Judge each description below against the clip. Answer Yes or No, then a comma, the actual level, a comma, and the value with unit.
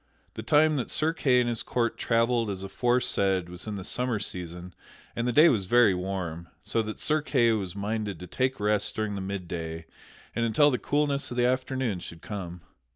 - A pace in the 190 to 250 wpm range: Yes, average, 200 wpm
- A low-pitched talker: Yes, low, 110 Hz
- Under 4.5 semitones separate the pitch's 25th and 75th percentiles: No, average, 4.8 semitones